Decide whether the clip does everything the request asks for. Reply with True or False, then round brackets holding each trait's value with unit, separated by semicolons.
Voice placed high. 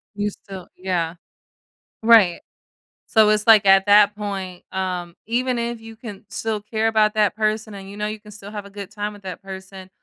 True (205 Hz)